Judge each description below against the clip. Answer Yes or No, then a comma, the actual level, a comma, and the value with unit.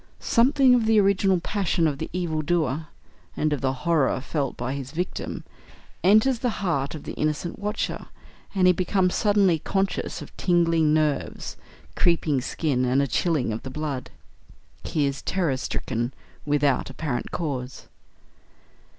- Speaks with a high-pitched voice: No, medium, 160 Hz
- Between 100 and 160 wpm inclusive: Yes, average, 150 wpm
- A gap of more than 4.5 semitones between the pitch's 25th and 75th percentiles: Yes, average, 5.1 semitones